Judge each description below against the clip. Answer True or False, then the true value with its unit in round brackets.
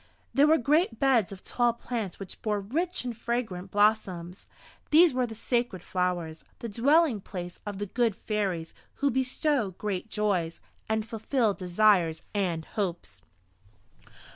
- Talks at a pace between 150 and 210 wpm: False (140 wpm)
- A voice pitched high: True (215 Hz)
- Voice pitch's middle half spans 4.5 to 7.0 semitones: True (4.9 semitones)